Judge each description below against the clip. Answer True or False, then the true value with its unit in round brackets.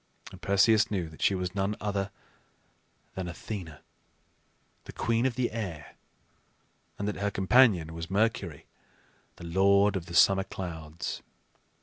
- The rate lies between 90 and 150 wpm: True (135 wpm)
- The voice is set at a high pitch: False (95 Hz)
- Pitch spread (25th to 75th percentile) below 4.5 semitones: True (3.4 semitones)